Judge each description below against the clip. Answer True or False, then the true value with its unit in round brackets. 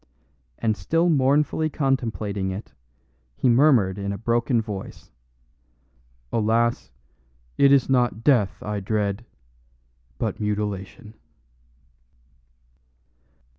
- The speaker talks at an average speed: False (90 wpm)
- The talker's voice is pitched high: False (115 Hz)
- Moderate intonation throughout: True (4.2 semitones)